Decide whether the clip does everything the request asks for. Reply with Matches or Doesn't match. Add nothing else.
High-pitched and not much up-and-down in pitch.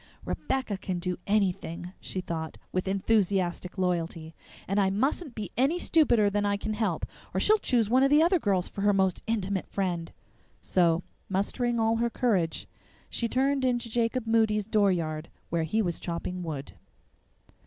Doesn't match